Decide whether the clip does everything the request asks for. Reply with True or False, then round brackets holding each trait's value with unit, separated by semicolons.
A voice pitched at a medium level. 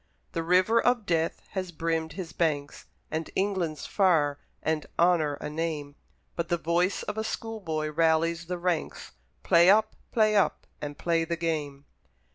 True (165 Hz)